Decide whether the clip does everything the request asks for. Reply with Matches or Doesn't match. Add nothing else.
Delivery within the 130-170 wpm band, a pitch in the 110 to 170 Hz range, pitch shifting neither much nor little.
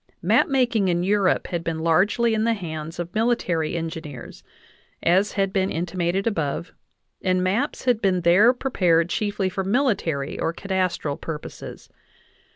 Doesn't match